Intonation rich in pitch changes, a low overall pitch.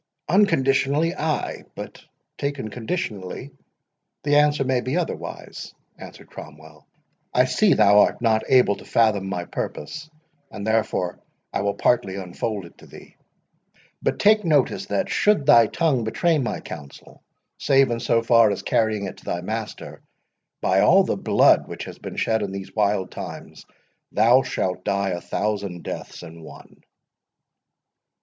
Yes: wide, 5.7 semitones; low, 110 Hz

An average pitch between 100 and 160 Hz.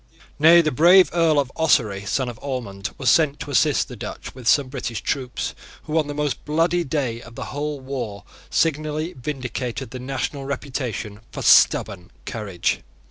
Yes: low, 135 Hz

